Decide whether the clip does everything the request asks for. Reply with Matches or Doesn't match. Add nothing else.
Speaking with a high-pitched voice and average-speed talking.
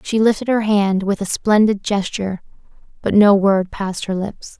Matches